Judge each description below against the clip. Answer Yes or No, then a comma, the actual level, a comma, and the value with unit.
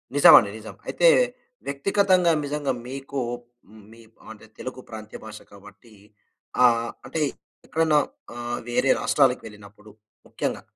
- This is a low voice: Yes, low, 125 Hz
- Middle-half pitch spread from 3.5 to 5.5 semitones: Yes, average, 4.6 semitones